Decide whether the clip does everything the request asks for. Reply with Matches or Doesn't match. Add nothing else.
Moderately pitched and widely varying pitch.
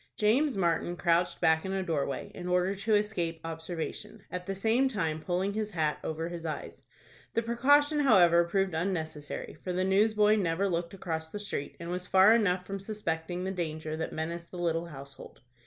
Doesn't match